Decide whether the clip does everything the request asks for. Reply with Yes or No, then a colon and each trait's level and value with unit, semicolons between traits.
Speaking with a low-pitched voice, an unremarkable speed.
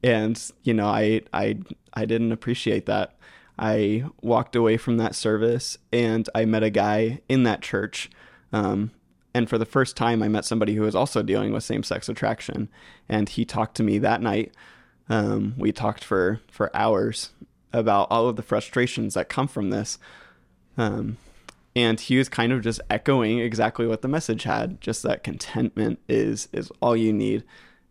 Yes: low, 110 Hz; average, 180 wpm